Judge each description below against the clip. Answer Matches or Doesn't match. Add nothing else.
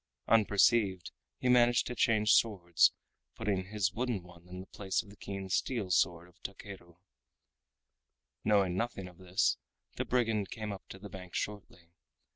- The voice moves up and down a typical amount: Matches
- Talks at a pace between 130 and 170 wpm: Matches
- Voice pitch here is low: Matches